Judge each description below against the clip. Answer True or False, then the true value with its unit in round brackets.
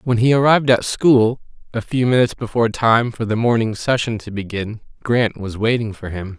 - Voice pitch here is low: True (115 Hz)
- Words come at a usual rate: True (195 wpm)